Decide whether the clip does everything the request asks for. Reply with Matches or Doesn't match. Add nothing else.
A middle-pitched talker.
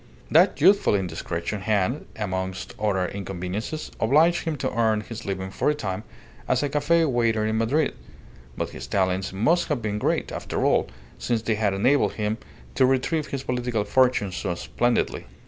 Doesn't match